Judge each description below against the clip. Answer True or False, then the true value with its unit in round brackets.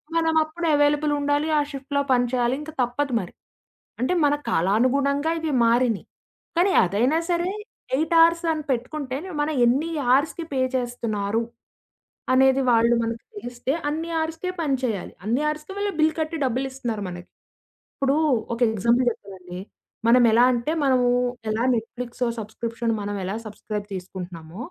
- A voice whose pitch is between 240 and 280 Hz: True (255 Hz)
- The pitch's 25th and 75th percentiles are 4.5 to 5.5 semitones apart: True (4.8 semitones)